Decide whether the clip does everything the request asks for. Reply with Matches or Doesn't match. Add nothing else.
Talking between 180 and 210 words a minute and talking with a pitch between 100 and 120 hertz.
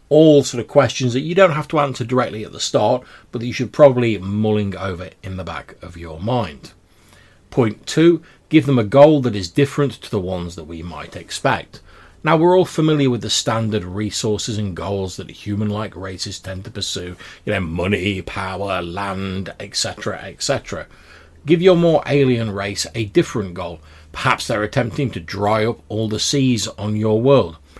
Matches